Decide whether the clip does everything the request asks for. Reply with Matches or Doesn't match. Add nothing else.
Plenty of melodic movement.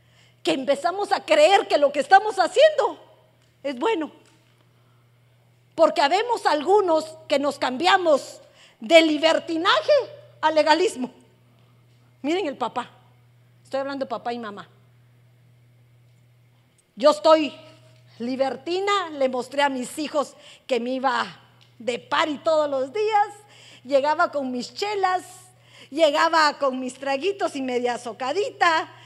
Matches